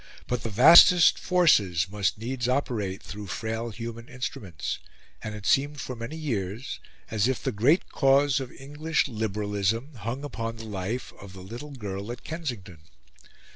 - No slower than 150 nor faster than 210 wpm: Yes, average, 155 wpm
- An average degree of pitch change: Yes, average, 4.8 semitones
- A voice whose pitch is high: No, low, 115 Hz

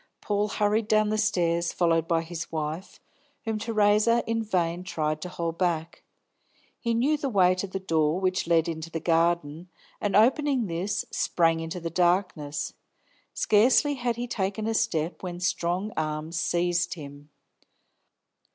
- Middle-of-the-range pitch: Yes, medium, 180 Hz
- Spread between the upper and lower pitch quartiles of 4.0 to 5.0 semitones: Yes, average, 4.4 semitones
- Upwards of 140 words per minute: Yes, average, 150 wpm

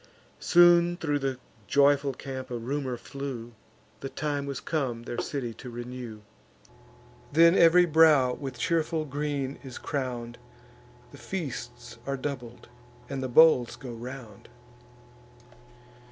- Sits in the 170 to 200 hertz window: No, low, 135 Hz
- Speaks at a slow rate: Yes, slow, 125 wpm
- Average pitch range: Yes, average, 3.4 semitones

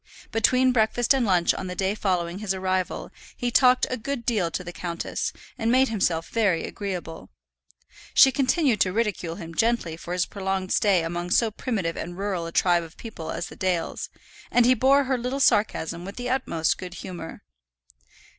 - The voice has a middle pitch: No, high, 195 Hz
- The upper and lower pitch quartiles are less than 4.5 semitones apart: No, wide, 5.4 semitones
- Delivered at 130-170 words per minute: No, average, 185 wpm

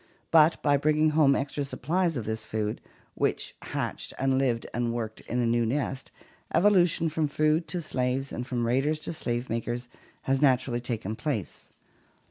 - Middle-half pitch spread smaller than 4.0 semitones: No, average, 4.3 semitones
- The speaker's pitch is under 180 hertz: Yes, low, 135 Hz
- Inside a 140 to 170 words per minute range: Yes, average, 165 wpm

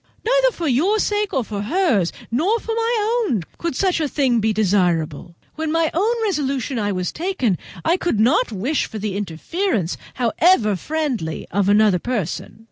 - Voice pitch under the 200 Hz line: No, very high, 260 Hz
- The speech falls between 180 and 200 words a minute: No, average, 165 wpm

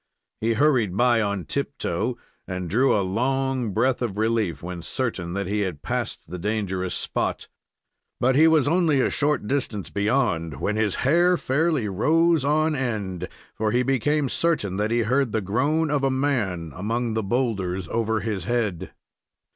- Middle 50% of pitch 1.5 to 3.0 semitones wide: No, wide, 5.5 semitones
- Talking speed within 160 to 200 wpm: Yes, average, 165 wpm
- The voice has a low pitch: Yes, low, 115 Hz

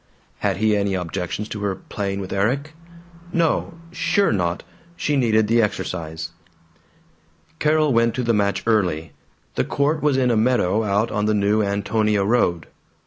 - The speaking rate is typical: Yes, average, 155 wpm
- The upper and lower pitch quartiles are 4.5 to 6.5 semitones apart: No, average, 3.7 semitones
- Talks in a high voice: No, low, 105 Hz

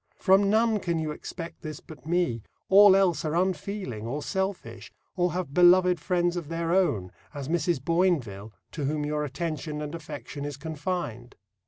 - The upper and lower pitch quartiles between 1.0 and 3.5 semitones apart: No, average, 3.9 semitones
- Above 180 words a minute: No, average, 165 wpm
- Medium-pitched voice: Yes, medium, 165 Hz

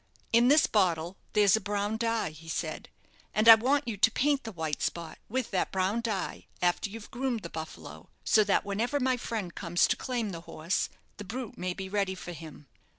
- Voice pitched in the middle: No, high, 205 Hz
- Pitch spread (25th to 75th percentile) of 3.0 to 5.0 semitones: Yes, average, 4.6 semitones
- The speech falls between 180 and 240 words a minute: Yes, fast, 205 wpm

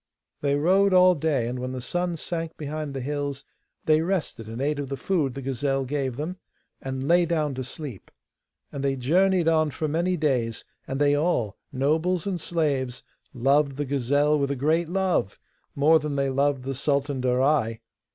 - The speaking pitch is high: No, medium, 145 Hz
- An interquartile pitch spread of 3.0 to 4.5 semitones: Yes, average, 3.3 semitones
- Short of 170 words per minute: No, average, 180 wpm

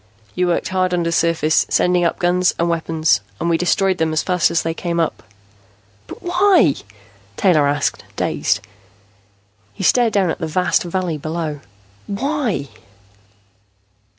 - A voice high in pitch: No, medium, 170 Hz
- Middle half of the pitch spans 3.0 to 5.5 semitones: No, narrow, 2.5 semitones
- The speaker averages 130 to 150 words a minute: Yes, average, 140 wpm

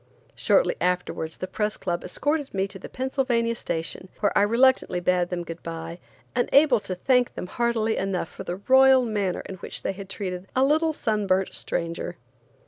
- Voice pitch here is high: Yes, high, 200 Hz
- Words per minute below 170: No, average, 180 wpm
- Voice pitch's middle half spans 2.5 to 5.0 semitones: No, wide, 5.6 semitones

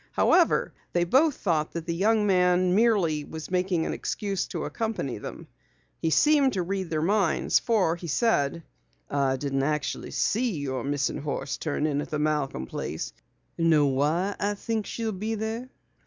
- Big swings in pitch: Yes, wide, 5.8 semitones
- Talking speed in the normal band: Yes, average, 170 wpm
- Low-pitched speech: No, medium, 175 Hz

